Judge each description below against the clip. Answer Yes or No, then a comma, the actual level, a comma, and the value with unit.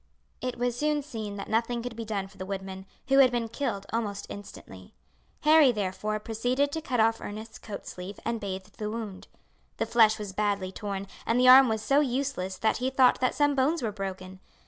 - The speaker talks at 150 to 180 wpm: No, fast, 205 wpm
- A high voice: Yes, high, 220 Hz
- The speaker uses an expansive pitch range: No, average, 4.1 semitones